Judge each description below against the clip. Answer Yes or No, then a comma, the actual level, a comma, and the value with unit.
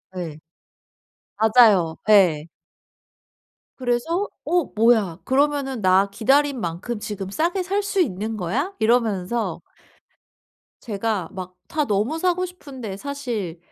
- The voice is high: Yes, high, 225 Hz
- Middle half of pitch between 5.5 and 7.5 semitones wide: Yes, wide, 6.7 semitones